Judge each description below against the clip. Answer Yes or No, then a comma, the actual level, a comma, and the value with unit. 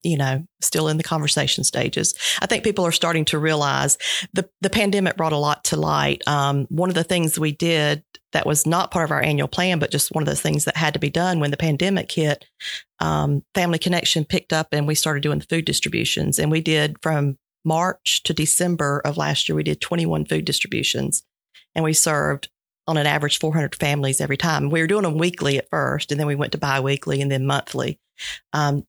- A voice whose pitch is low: No, medium, 155 Hz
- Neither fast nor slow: No, fast, 225 wpm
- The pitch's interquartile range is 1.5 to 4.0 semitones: Yes, narrow, 2.6 semitones